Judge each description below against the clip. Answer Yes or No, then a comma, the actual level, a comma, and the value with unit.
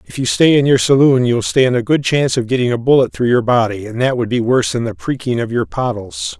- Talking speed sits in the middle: No, fast, 270 wpm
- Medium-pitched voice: No, low, 125 Hz